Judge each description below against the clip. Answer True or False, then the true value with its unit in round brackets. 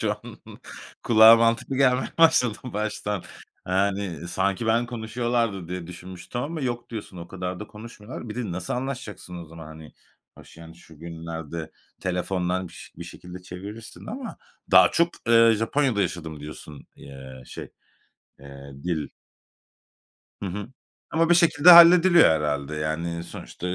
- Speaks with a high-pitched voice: False (95 Hz)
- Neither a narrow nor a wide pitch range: False (6.1 semitones)